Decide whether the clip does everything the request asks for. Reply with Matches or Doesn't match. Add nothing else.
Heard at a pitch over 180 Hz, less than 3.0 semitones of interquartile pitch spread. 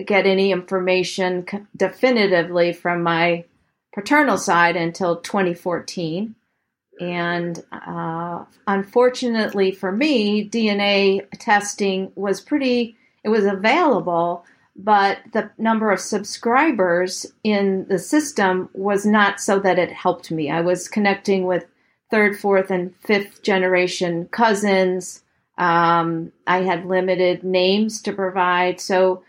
Matches